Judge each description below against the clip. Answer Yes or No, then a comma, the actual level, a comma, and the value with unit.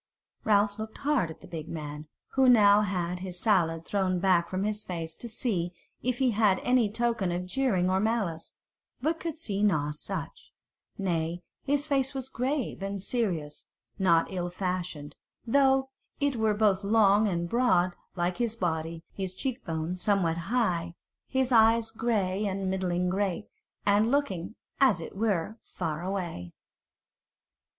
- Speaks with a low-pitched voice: No, high, 195 Hz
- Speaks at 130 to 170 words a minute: Yes, average, 155 wpm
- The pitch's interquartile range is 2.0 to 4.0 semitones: No, average, 4.8 semitones